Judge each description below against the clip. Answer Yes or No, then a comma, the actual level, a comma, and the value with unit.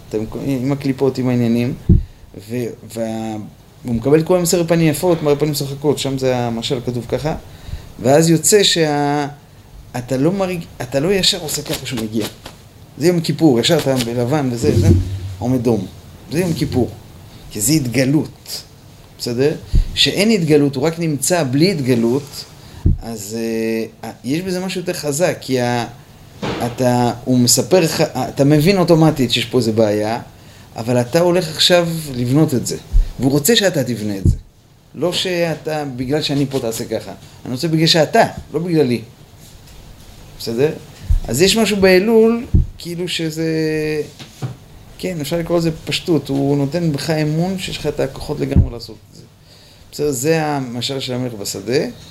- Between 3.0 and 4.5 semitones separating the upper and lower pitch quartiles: No, average, 5.2 semitones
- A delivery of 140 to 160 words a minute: Yes, fast, 150 wpm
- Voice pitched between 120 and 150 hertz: Yes, medium, 140 Hz